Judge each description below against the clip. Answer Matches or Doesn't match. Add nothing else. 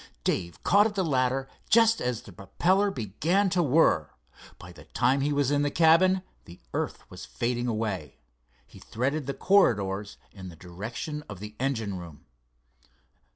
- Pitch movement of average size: Doesn't match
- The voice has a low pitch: Matches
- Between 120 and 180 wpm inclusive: Matches